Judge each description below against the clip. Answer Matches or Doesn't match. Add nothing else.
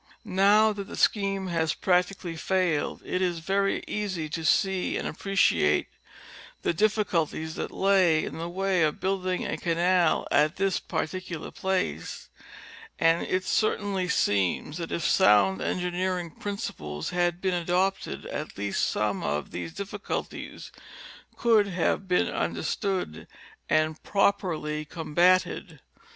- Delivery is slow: Matches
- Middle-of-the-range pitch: Matches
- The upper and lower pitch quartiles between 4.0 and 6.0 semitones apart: Doesn't match